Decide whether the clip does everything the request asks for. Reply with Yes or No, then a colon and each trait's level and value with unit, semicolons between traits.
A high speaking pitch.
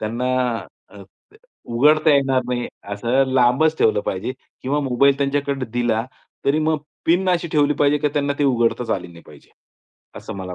No: low, 135 Hz